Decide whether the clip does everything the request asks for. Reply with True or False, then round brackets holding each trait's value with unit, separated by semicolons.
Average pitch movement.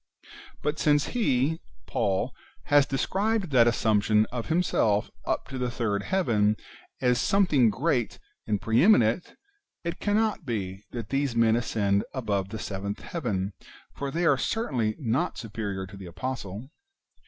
False (6.0 semitones)